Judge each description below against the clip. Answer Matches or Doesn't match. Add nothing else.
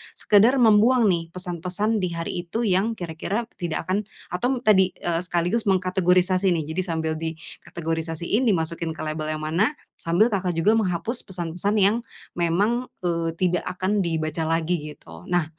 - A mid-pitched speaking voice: Matches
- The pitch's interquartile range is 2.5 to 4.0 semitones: Matches